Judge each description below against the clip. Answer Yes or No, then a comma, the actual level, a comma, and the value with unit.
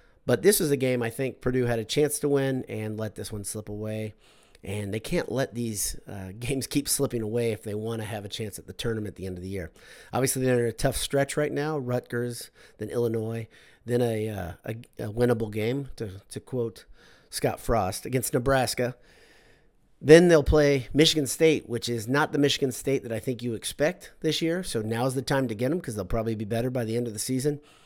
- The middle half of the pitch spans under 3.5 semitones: No, average, 3.8 semitones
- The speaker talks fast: Yes, fast, 230 wpm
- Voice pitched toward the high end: No, low, 120 Hz